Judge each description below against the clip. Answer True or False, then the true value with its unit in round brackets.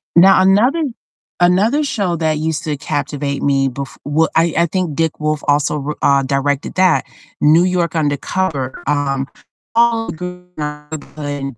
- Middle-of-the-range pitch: True (155 Hz)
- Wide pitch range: False (3.8 semitones)